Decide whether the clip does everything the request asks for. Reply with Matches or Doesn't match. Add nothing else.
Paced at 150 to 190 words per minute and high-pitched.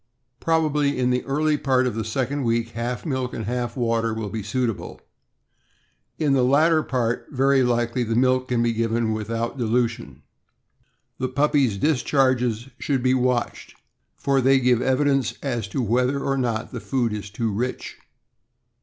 Doesn't match